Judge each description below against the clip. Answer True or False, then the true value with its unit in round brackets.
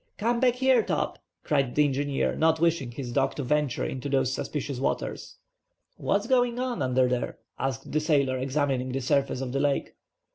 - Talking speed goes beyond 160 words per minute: True (180 wpm)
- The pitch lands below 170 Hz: True (140 Hz)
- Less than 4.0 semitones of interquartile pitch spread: True (3.5 semitones)